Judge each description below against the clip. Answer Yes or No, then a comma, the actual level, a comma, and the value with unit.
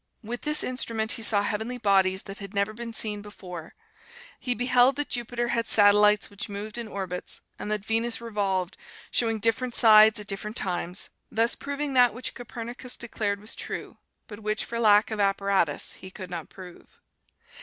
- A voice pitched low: No, high, 215 Hz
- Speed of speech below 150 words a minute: No, average, 175 wpm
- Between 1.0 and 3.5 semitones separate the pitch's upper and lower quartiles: Yes, average, 2.9 semitones